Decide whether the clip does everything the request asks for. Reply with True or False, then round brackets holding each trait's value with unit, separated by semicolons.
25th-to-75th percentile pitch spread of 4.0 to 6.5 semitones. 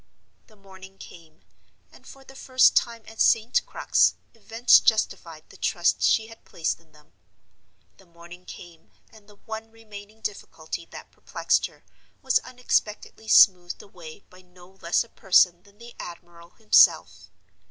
True (4.4 semitones)